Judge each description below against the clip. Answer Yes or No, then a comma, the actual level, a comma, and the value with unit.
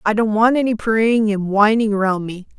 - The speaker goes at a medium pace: No, fast, 210 wpm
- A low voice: No, high, 215 Hz